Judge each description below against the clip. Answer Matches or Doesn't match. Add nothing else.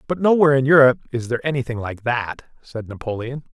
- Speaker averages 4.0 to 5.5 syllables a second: Doesn't match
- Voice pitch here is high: Doesn't match